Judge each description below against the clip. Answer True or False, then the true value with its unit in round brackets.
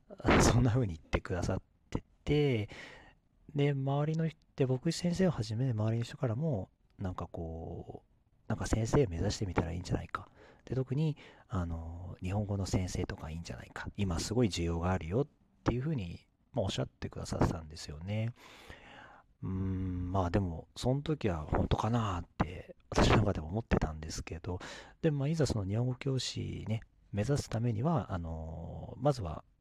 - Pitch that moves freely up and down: True (6.1 semitones)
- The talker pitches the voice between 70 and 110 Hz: True (105 Hz)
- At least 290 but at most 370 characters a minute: True (365 characters per minute)